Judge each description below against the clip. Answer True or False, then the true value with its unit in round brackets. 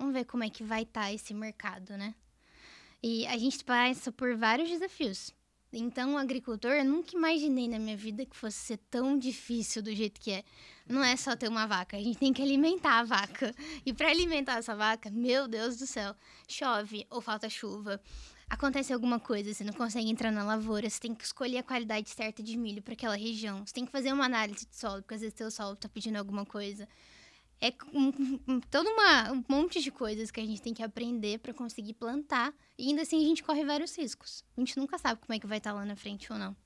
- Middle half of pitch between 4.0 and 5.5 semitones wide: False (3.6 semitones)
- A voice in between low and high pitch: False (235 Hz)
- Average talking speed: False (230 wpm)